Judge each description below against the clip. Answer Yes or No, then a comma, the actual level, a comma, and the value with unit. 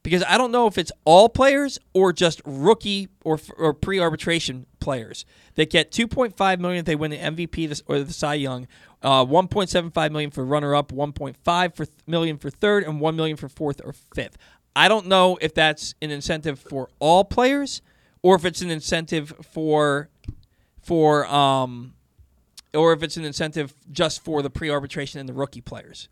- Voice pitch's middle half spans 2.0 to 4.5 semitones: Yes, average, 3.7 semitones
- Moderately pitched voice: Yes, medium, 155 Hz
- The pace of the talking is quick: No, average, 175 wpm